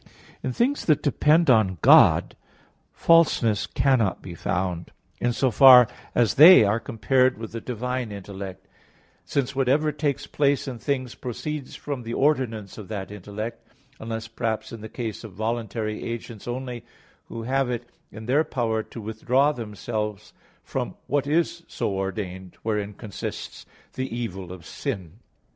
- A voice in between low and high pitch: No, low, 115 Hz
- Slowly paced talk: No, average, 150 wpm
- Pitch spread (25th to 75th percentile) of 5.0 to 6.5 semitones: No, average, 3.9 semitones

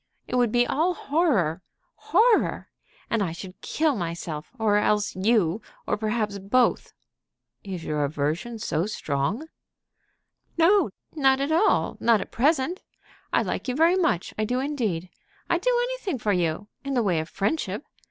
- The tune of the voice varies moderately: No, wide, 8.0 semitones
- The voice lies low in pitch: No, high, 225 Hz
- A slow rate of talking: No, average, 150 wpm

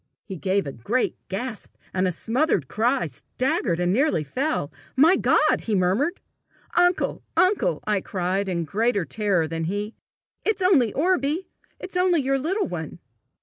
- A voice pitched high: Yes, high, 220 Hz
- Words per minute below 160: Yes, average, 150 wpm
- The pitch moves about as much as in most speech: No, wide, 8.9 semitones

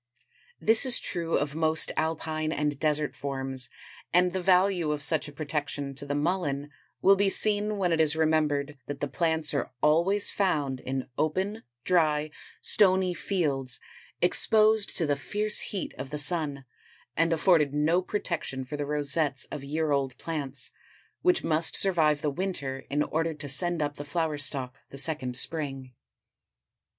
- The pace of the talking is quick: No, average, 160 wpm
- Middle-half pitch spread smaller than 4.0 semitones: Yes, average, 3.6 semitones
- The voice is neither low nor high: Yes, medium, 155 Hz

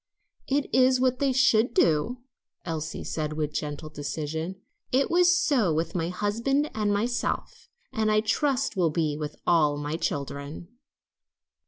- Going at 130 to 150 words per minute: Yes, average, 145 wpm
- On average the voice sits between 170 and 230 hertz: Yes, high, 190 Hz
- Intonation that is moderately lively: No, wide, 8.7 semitones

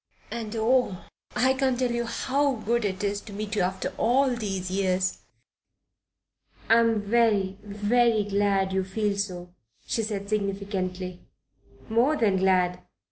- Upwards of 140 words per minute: No, slow, 135 wpm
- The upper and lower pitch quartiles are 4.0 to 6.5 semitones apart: No, average, 3.4 semitones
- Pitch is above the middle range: Yes, high, 205 Hz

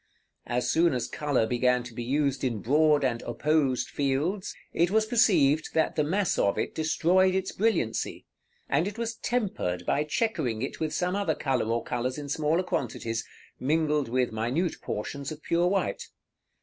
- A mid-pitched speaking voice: Yes, medium, 150 Hz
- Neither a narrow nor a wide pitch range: No, wide, 5.8 semitones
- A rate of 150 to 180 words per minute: Yes, average, 170 wpm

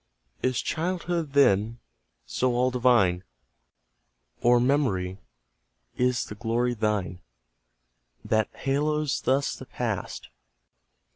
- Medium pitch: No, low, 125 Hz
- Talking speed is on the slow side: Yes, slow, 90 wpm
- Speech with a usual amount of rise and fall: Yes, average, 4.3 semitones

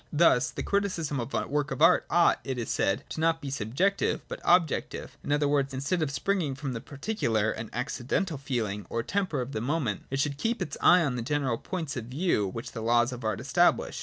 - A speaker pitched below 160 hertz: Yes, medium, 140 Hz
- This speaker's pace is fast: Yes, fast, 220 wpm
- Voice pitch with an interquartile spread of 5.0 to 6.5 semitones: Yes, wide, 5.4 semitones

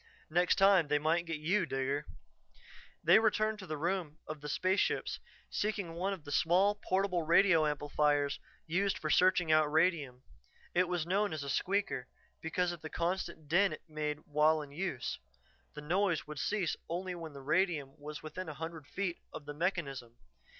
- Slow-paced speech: No, average, 170 wpm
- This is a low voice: No, medium, 165 Hz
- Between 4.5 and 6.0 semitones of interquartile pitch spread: No, average, 3.8 semitones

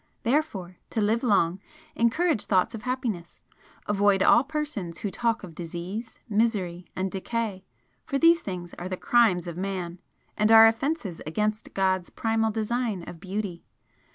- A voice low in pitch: No, high, 205 Hz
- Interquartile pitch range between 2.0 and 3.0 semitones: No, average, 4.1 semitones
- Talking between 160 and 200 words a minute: No, average, 150 wpm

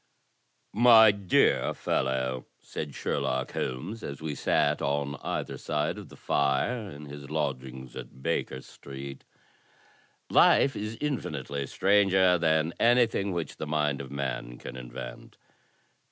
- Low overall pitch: Yes, very low, 75 Hz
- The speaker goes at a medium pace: No, slow, 125 wpm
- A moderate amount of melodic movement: No, wide, 6.3 semitones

